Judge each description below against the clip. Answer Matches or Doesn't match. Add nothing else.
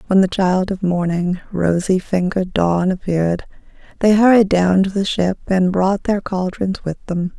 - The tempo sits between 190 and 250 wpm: Doesn't match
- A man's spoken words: Doesn't match